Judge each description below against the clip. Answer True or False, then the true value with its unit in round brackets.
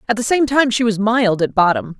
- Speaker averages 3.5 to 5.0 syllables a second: False (5.5 syllables/s)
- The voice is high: True (220 Hz)